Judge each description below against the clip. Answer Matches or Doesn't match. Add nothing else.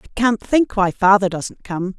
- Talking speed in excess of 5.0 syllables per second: Doesn't match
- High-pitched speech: Matches